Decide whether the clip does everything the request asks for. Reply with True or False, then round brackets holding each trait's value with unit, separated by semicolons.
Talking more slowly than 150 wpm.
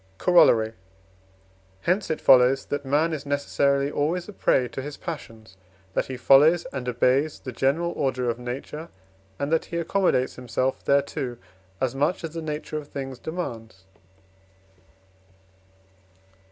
True (140 wpm)